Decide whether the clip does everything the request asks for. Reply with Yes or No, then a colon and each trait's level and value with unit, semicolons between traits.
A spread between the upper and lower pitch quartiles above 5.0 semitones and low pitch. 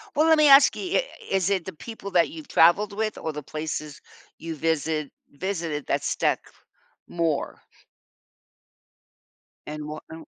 No: wide, 5.4 semitones; medium, 165 Hz